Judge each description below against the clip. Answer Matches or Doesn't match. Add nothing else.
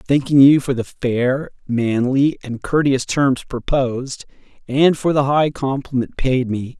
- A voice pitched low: Matches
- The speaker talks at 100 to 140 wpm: Doesn't match